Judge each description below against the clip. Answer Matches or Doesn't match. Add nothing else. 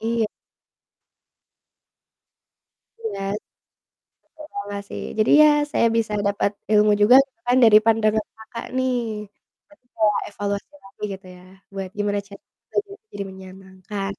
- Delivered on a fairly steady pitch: Matches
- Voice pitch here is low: Doesn't match